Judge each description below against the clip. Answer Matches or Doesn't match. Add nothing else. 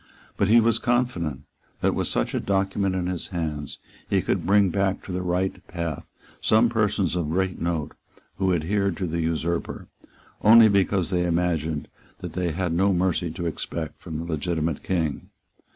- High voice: Doesn't match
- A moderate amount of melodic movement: Matches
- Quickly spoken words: Doesn't match